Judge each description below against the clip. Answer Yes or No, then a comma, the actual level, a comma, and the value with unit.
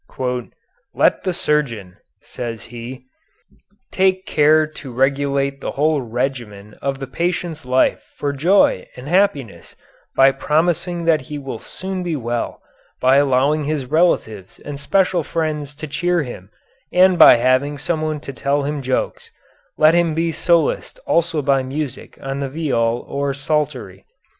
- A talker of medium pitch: Yes, medium, 145 Hz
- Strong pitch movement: No, average, 3.6 semitones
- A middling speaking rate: Yes, average, 145 wpm